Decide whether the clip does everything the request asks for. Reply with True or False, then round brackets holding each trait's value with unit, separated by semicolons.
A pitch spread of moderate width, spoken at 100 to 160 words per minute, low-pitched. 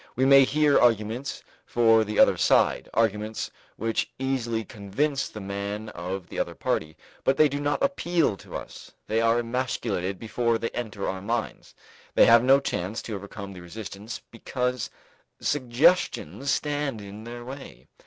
True (4.5 semitones; 155 wpm; 115 Hz)